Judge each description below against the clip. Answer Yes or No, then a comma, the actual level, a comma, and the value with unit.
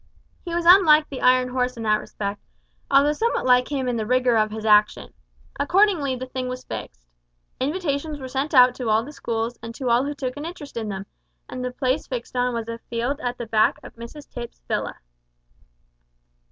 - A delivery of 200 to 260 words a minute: Yes, fast, 205 wpm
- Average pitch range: Yes, average, 3.5 semitones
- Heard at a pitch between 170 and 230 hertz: No, very high, 255 Hz